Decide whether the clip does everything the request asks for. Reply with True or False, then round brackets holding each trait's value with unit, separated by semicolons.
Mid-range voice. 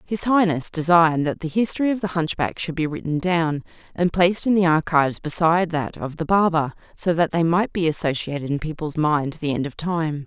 True (165 Hz)